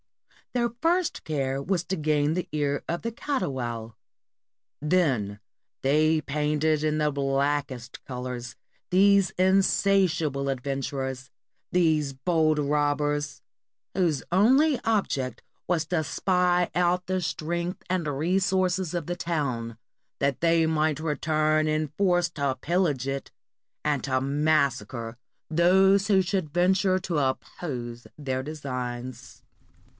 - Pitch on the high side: No, medium, 155 Hz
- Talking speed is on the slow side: Yes, slow, 120 wpm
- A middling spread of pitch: Yes, average, 4.5 semitones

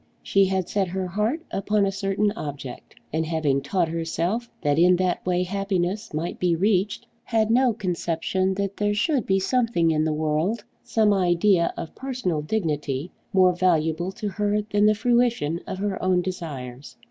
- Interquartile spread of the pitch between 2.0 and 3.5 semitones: No, average, 3.9 semitones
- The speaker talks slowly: No, average, 170 wpm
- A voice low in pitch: No, medium, 185 Hz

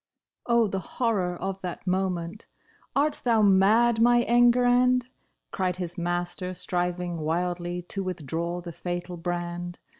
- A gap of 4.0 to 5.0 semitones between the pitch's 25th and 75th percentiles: Yes, average, 4.3 semitones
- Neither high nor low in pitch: Yes, medium, 180 Hz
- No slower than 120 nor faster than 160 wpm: Yes, average, 145 wpm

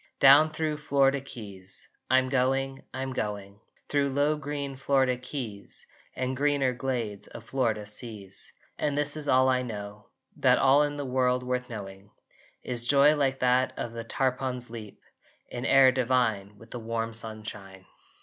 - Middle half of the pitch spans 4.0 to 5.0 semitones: No, average, 3.4 semitones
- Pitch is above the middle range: No, low, 125 Hz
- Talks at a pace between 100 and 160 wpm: Yes, average, 155 wpm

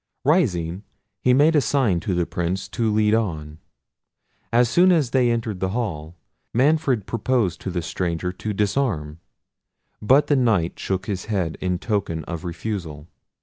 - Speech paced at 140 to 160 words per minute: Yes, average, 155 wpm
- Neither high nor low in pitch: No, low, 100 Hz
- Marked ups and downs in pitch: Yes, wide, 5.9 semitones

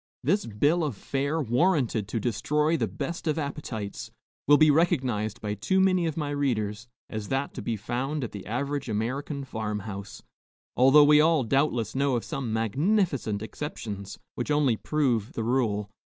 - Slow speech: No, average, 170 wpm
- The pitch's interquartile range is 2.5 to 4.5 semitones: No, wide, 5.5 semitones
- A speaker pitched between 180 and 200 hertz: No, low, 135 Hz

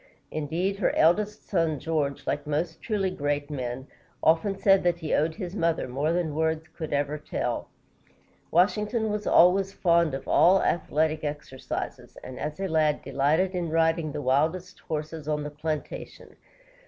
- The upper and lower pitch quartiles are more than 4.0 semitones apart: No, average, 3.3 semitones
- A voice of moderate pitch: Yes, medium, 160 Hz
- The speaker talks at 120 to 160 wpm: Yes, average, 155 wpm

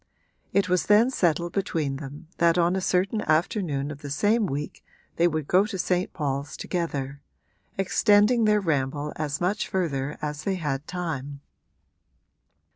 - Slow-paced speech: No, average, 150 wpm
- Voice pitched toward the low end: No, medium, 170 Hz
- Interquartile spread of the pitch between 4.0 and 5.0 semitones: Yes, average, 4.7 semitones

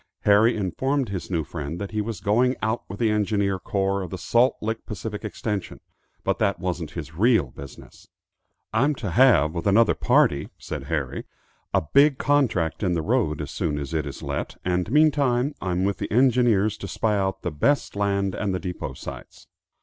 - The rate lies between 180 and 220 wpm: Yes, average, 190 wpm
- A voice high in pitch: No, low, 100 Hz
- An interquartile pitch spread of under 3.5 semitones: No, average, 4.6 semitones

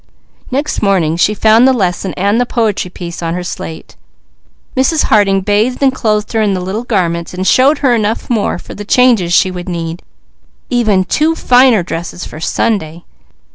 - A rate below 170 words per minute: No, average, 175 wpm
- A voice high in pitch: Yes, high, 205 Hz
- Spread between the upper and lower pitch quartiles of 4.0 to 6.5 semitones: Yes, average, 5.2 semitones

